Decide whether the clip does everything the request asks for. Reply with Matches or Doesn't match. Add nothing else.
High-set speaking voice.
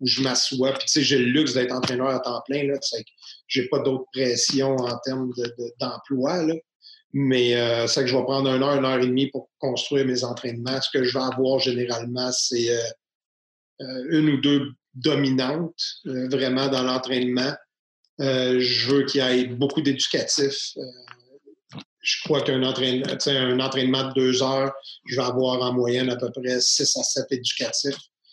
Doesn't match